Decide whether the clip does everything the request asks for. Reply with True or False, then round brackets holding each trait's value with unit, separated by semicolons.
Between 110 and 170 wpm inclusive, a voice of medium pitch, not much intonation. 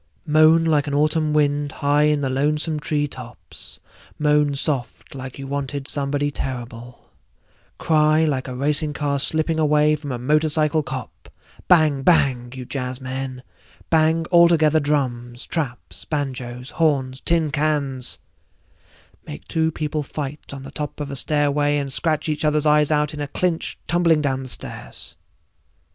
True (145 wpm; 145 Hz; 2.3 semitones)